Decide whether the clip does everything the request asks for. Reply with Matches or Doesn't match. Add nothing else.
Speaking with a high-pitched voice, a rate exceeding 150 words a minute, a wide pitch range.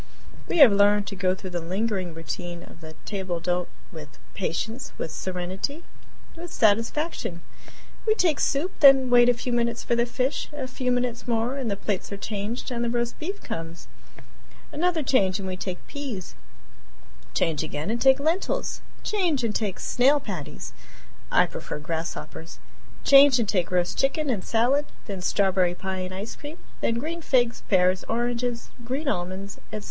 Matches